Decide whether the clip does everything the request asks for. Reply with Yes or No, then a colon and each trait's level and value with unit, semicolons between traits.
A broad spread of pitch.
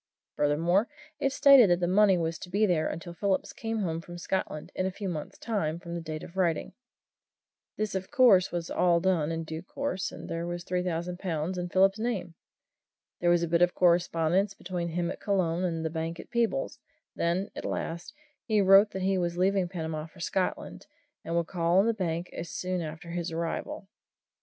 No: narrow, 2.4 semitones